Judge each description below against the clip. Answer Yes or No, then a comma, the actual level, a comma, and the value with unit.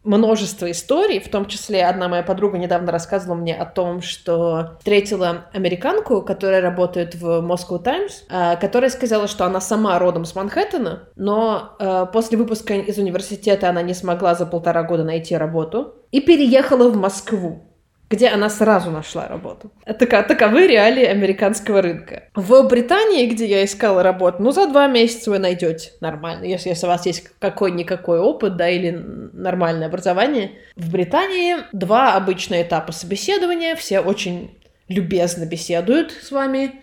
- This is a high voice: Yes, high, 195 Hz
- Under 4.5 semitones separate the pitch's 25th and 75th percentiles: Yes, average, 4.1 semitones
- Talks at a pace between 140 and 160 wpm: Yes, average, 150 wpm